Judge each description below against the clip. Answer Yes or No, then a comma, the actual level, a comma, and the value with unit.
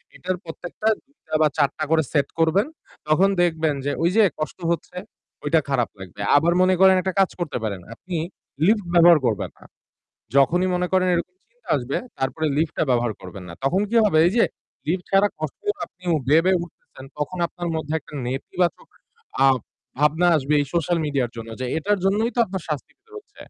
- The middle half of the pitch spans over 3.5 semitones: Yes, average, 4.5 semitones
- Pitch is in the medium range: Yes, medium, 165 Hz